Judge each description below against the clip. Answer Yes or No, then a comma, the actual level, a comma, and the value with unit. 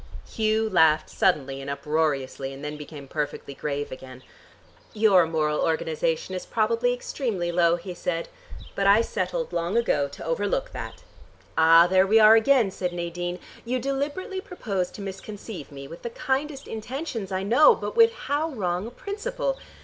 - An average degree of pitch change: No, wide, 6.8 semitones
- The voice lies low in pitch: No, high, 190 Hz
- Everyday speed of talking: Yes, average, 160 wpm